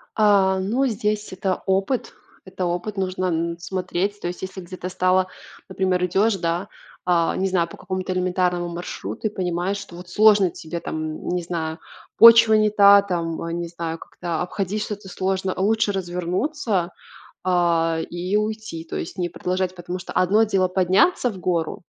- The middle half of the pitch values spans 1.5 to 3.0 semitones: Yes, narrow, 2.4 semitones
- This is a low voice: No, medium, 185 Hz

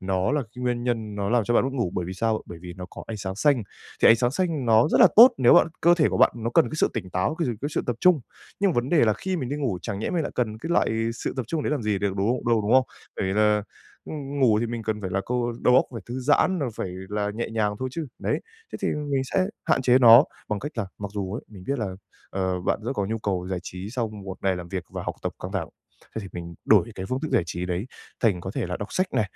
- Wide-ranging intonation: No, average, 5.0 semitones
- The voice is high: No, low, 115 Hz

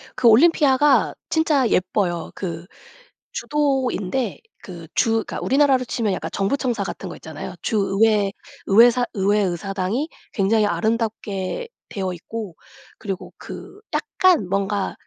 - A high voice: Yes, high, 215 Hz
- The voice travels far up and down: No, average, 5.0 semitones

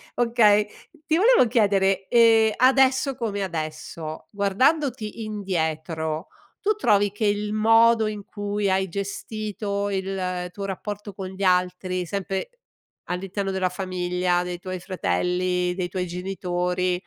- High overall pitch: Yes, high, 195 Hz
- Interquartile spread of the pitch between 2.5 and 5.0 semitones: Yes, average, 2.9 semitones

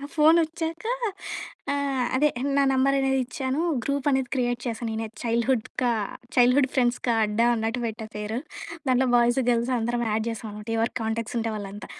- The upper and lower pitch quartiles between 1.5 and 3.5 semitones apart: Yes, average, 2.9 semitones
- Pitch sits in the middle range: No, high, 245 Hz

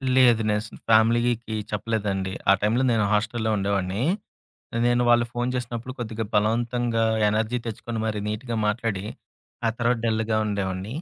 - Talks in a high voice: No, low, 110 Hz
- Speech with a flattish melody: Yes, narrow, 2.1 semitones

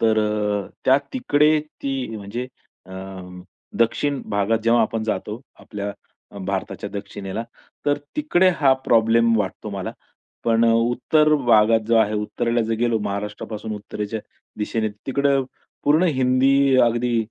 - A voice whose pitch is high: No, low, 115 Hz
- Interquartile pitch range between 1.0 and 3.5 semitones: No, average, 4.0 semitones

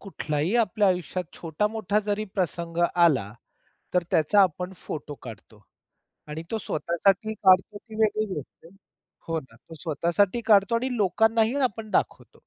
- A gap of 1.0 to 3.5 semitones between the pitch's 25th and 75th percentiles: No, average, 4.9 semitones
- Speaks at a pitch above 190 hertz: No, medium, 185 Hz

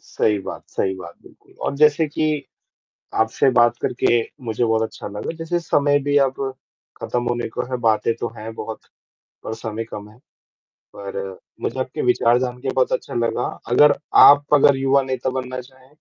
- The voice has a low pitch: Yes, low, 125 Hz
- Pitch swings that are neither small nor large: Yes, average, 3.6 semitones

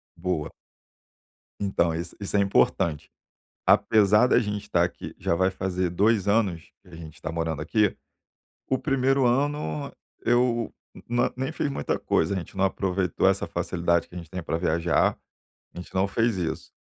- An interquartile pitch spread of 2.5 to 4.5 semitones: No, average, 4.9 semitones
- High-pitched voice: No, very low, 95 Hz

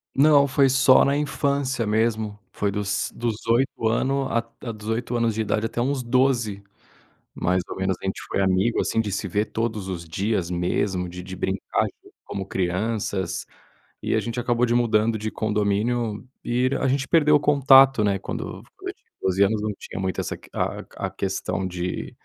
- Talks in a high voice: No, low, 110 Hz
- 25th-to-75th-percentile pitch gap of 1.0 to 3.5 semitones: No, average, 4.1 semitones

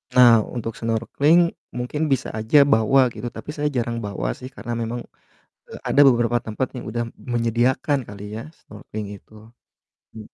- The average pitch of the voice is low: Yes, low, 120 Hz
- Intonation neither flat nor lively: Yes, average, 3.1 semitones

